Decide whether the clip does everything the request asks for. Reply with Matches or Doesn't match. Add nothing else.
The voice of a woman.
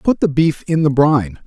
Doesn't match